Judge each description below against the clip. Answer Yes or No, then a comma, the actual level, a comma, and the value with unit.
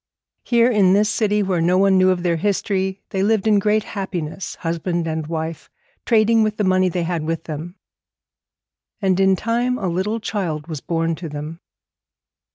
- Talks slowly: No, average, 175 wpm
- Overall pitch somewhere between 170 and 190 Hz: Yes, medium, 185 Hz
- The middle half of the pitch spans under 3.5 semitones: No, average, 4.0 semitones